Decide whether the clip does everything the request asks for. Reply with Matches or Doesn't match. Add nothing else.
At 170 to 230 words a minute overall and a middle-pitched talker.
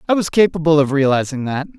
Matches